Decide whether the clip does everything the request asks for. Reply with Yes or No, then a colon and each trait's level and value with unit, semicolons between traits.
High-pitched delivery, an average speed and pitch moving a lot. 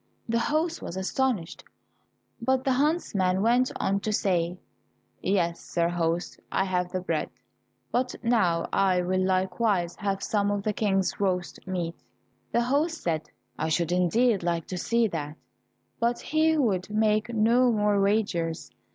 No: high, 195 Hz; average, 150 wpm; average, 4.7 semitones